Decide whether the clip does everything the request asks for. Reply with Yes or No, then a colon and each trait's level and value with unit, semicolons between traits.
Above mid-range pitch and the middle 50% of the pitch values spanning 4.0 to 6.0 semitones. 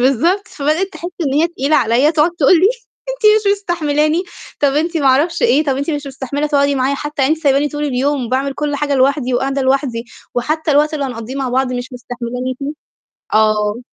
No: very high, 280 Hz; average, 2.9 semitones